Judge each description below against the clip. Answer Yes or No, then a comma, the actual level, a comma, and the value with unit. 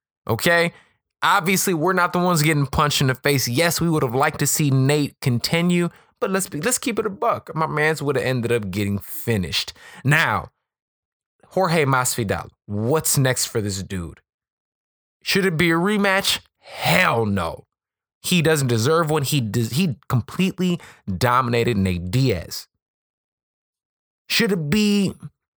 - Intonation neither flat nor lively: No, wide, 6.8 semitones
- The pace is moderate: Yes, average, 155 wpm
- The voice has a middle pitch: Yes, medium, 150 Hz